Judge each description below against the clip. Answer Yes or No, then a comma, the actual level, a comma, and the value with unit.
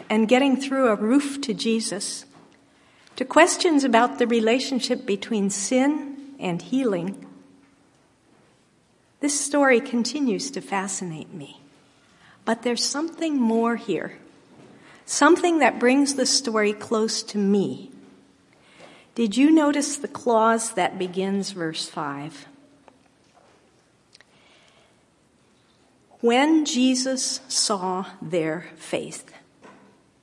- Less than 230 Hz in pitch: No, high, 235 Hz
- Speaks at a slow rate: Yes, slow, 95 wpm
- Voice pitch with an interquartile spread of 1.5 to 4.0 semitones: No, average, 5.2 semitones